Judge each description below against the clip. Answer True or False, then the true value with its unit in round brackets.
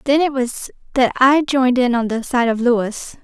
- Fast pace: True (225 wpm)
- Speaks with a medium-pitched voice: False (255 Hz)